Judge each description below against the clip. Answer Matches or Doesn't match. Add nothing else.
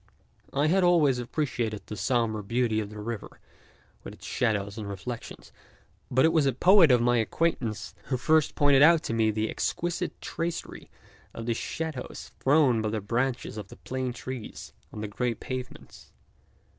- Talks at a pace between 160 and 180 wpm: Matches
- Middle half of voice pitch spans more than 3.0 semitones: Matches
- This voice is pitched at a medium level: Doesn't match